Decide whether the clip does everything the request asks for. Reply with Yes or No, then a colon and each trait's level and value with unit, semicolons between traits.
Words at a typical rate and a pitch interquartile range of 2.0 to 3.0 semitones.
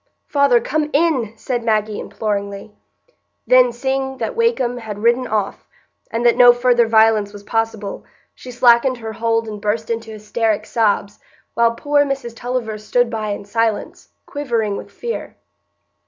Yes: average, 150 wpm; average, 2.7 semitones